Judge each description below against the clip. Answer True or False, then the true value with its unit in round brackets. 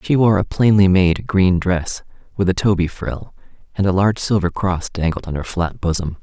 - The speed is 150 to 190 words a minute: False (200 wpm)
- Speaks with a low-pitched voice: True (95 Hz)